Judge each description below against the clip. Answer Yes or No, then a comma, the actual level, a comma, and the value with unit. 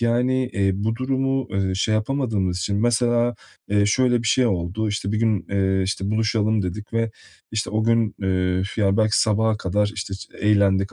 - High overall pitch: No, low, 105 Hz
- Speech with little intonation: No, average, 3.0 semitones